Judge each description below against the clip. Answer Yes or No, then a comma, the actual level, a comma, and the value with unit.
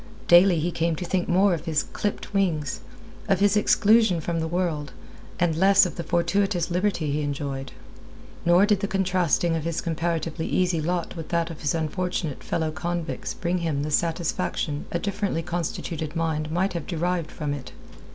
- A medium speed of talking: Yes, average, 175 wpm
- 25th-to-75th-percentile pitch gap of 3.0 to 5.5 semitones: No, narrow, 2.4 semitones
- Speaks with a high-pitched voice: No, medium, 170 Hz